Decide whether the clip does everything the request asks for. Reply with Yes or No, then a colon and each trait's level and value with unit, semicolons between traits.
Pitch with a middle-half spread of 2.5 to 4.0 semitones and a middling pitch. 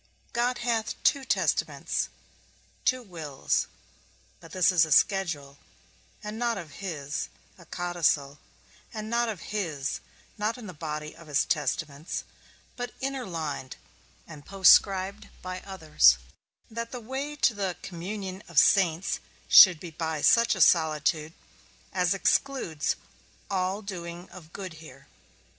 No: average, 5.2 semitones; medium, 180 Hz